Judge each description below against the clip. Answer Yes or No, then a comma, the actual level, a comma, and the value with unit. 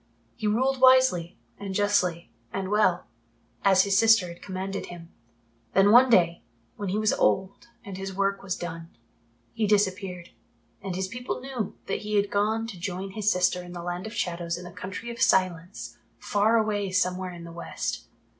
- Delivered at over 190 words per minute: No, average, 180 wpm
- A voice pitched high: Yes, high, 195 Hz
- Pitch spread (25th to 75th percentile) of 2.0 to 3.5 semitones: Yes, average, 2.9 semitones